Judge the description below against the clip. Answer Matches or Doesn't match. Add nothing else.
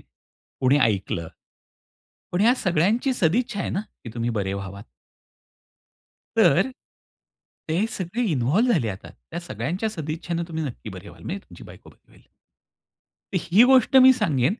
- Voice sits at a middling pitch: Matches